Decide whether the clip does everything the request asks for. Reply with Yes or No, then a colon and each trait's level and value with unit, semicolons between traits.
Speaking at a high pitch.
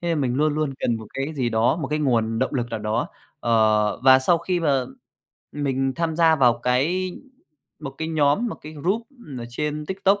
No: medium, 145 Hz